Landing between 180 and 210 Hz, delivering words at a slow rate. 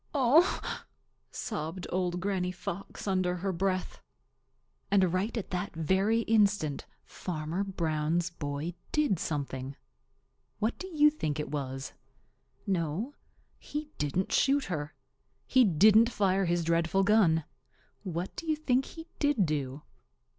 Yes: medium, 185 Hz; slow, 125 wpm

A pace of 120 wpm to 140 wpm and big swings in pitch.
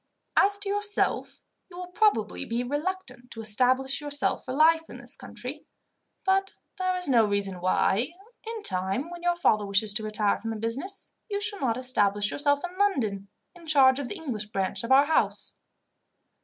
No: average, 175 wpm; wide, 8.7 semitones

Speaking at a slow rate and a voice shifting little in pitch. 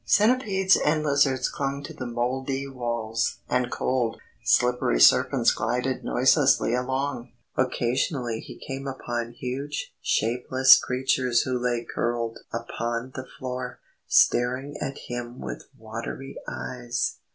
Yes: slow, 120 wpm; narrow, 2.1 semitones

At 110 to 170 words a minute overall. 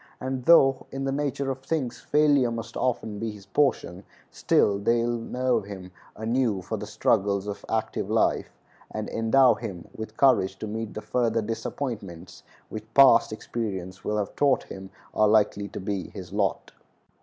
Yes: average, 165 wpm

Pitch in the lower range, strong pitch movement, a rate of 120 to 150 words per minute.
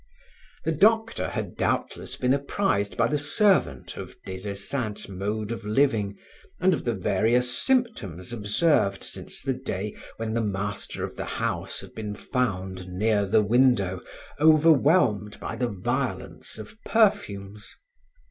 Yes: low, 110 Hz; wide, 5.9 semitones; average, 140 wpm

